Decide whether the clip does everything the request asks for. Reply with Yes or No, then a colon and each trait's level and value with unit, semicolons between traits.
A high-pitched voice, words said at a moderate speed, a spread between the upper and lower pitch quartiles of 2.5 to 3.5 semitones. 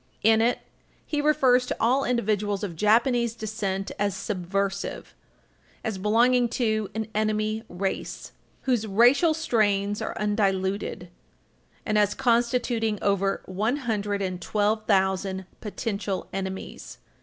No: high, 210 Hz; slow, 110 wpm; average, 3.0 semitones